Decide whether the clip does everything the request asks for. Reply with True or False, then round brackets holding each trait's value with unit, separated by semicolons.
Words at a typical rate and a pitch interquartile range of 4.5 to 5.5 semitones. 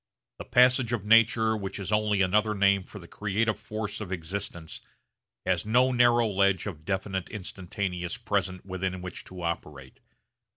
False (155 wpm; 3.0 semitones)